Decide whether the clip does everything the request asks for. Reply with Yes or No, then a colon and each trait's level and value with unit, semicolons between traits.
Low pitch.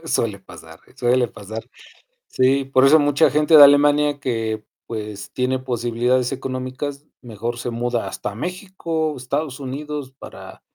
Yes: low, 130 Hz